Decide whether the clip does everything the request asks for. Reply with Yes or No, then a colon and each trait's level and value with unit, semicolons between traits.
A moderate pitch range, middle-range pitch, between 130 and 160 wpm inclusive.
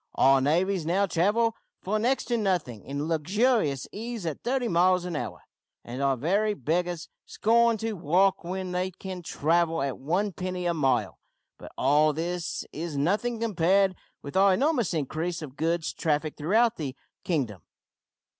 Yes: average, 4.6 semitones; medium, 175 Hz; average, 155 wpm